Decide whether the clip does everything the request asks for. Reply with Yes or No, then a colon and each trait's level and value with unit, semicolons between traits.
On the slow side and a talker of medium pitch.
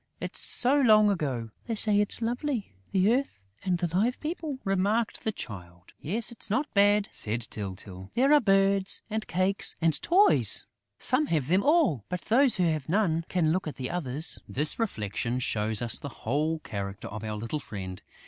No: average, 180 wpm; medium, 180 Hz